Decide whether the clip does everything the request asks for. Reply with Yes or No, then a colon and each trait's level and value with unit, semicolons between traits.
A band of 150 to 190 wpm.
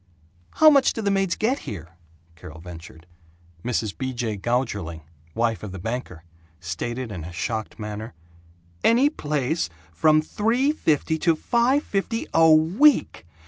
No: average, 140 wpm